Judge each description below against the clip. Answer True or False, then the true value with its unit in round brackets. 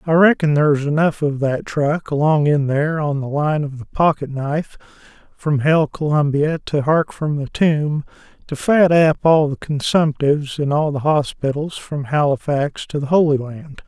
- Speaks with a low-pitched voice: False (150 Hz)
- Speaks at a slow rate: False (175 wpm)